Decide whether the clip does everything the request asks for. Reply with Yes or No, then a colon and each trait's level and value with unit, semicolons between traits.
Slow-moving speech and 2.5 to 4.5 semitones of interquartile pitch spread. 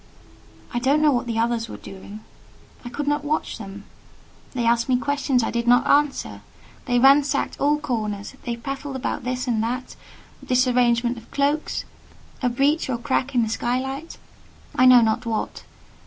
No: average, 170 wpm; average, 2.9 semitones